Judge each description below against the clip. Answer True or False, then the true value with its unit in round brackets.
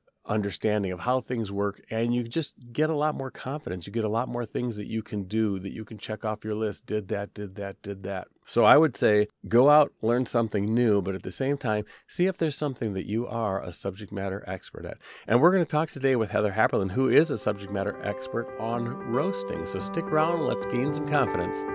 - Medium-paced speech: False (235 wpm)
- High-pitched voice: False (110 Hz)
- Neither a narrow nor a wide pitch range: True (4.3 semitones)